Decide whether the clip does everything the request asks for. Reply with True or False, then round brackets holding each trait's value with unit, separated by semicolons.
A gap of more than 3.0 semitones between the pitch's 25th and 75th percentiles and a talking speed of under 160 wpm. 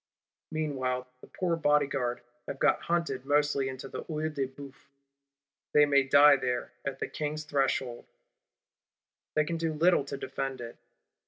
False (2.4 semitones; 150 wpm)